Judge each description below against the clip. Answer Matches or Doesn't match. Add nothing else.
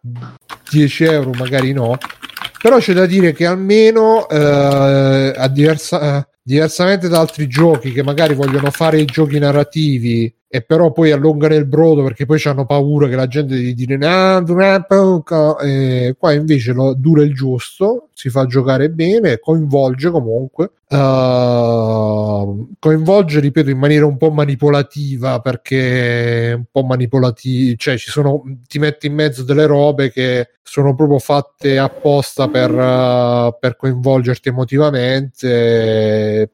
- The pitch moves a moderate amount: Matches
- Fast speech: Doesn't match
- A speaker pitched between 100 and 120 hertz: Doesn't match